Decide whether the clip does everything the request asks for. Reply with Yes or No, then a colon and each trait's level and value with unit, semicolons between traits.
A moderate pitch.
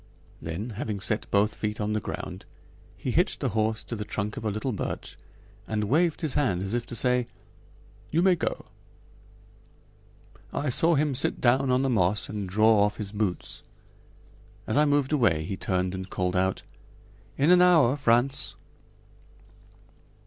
No: low, 110 Hz